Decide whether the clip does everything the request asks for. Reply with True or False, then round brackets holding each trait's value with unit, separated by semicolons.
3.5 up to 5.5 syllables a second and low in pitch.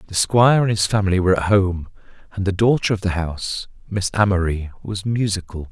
False (5.9 syllables/s; 100 Hz)